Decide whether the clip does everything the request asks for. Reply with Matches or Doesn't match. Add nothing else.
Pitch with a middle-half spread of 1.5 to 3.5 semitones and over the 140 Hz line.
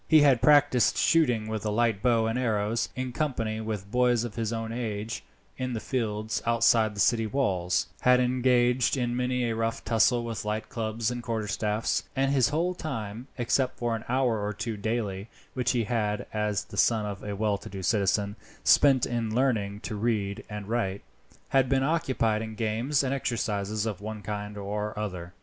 Doesn't match